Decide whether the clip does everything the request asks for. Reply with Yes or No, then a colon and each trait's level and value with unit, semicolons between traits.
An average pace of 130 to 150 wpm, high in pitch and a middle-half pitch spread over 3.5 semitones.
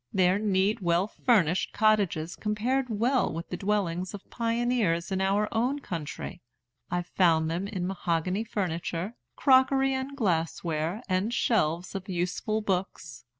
Yes: average, 140 wpm; high, 195 Hz; average, 4.4 semitones